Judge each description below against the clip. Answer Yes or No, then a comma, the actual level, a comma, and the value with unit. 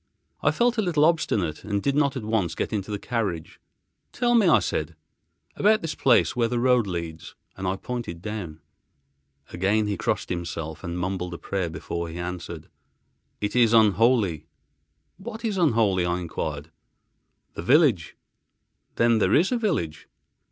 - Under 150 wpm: No, average, 160 wpm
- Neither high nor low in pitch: No, low, 105 Hz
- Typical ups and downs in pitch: No, wide, 7.1 semitones